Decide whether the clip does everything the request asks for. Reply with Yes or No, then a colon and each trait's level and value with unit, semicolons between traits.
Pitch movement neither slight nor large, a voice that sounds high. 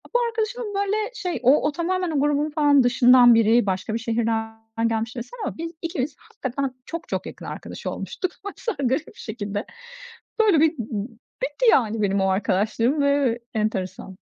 No: wide, 7.1 semitones; very high, 265 Hz